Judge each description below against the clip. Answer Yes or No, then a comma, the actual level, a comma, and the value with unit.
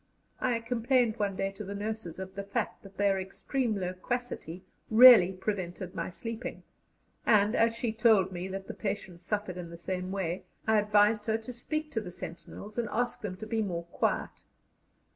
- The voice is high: Yes, high, 205 Hz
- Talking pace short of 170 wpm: No, average, 180 wpm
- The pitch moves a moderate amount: Yes, average, 3.3 semitones